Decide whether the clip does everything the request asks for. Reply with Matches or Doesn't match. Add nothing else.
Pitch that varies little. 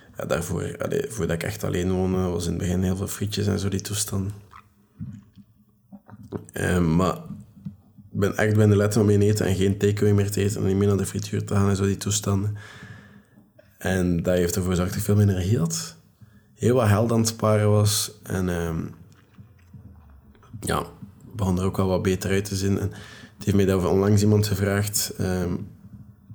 Matches